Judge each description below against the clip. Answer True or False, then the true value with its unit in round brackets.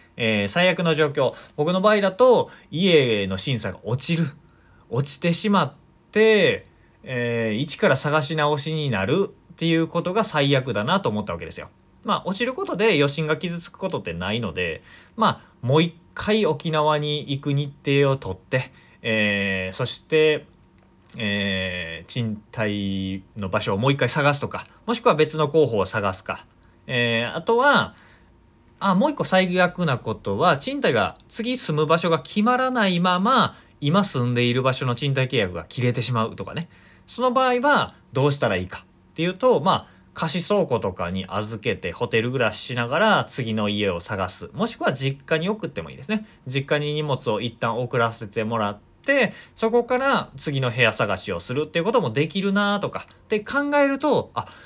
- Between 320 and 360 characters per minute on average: True (330 characters per minute)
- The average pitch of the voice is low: False (145 Hz)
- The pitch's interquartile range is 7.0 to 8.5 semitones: True (7.9 semitones)